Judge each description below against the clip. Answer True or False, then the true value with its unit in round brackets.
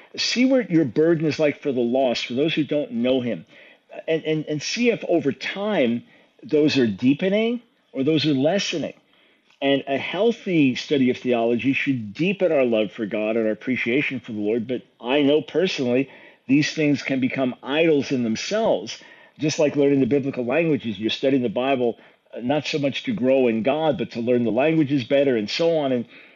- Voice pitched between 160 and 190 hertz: False (140 Hz)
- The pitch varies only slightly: False (3.9 semitones)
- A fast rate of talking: False (195 wpm)